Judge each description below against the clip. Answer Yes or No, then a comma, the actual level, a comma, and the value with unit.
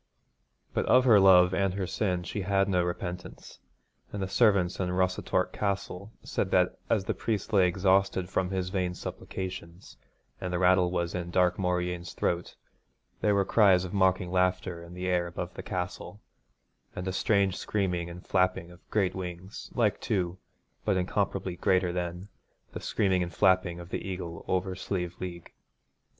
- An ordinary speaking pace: Yes, average, 165 wpm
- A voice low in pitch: Yes, very low, 90 Hz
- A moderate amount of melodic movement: No, narrow, 1.5 semitones